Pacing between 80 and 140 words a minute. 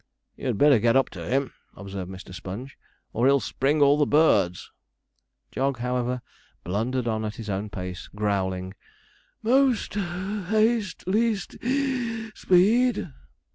Yes: slow, 135 wpm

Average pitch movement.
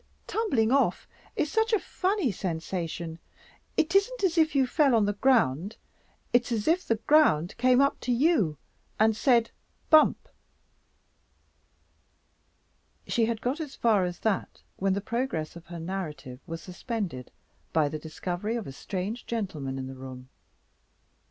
No: wide, 8.2 semitones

